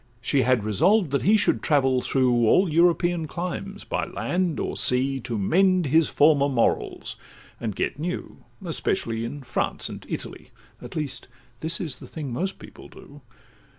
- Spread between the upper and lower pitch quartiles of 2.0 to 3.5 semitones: No, wide, 5.4 semitones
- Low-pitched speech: No, medium, 150 Hz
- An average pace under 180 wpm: Yes, average, 160 wpm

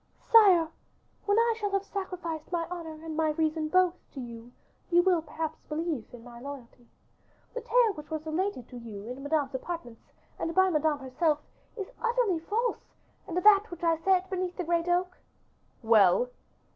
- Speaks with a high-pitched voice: Yes, very high, 330 Hz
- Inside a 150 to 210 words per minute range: Yes, average, 175 wpm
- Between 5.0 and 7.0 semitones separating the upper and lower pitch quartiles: No, average, 4.4 semitones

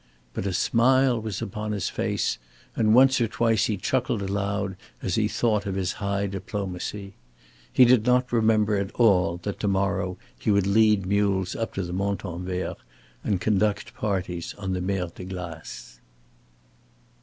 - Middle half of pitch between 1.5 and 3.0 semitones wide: Yes, narrow, 2.5 semitones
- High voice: No, low, 100 Hz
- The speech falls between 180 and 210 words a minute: No, average, 160 wpm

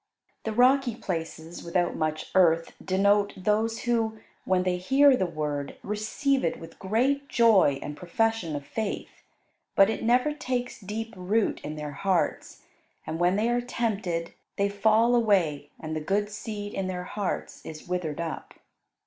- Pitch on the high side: Yes, high, 200 Hz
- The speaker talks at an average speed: Yes, average, 155 wpm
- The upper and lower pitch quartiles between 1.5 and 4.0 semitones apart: No, average, 5.0 semitones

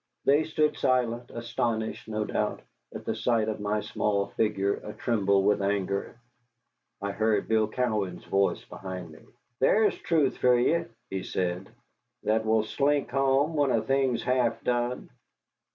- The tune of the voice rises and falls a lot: No, average, 4.0 semitones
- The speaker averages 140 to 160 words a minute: Yes, average, 150 wpm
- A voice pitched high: No, low, 110 Hz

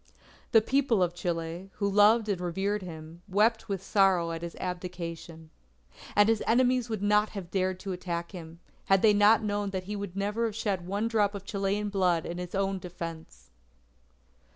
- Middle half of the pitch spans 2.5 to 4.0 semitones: Yes, average, 3.0 semitones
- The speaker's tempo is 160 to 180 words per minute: Yes, average, 175 wpm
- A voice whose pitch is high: Yes, high, 195 Hz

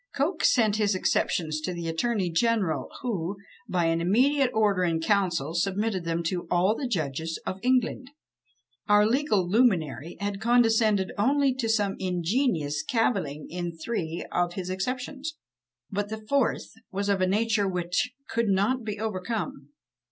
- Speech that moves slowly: No, average, 150 wpm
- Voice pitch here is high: Yes, high, 200 Hz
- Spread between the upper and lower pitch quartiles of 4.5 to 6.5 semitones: Yes, average, 4.9 semitones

